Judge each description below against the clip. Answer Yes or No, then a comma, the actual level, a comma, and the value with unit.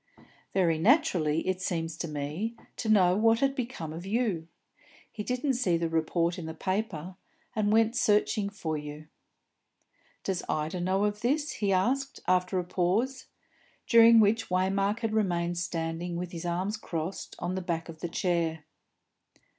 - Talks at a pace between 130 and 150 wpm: No, average, 160 wpm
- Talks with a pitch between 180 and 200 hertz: Yes, medium, 185 Hz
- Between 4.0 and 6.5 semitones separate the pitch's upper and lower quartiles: Yes, average, 4.6 semitones